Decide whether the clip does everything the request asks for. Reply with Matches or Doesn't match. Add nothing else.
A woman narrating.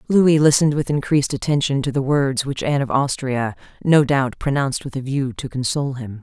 Matches